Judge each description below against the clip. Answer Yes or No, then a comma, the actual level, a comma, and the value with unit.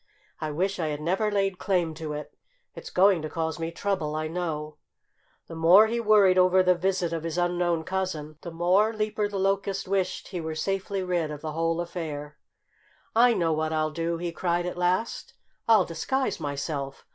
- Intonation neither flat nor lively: Yes, average, 3.3 semitones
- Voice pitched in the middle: Yes, medium, 175 Hz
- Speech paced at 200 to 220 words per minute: No, average, 190 wpm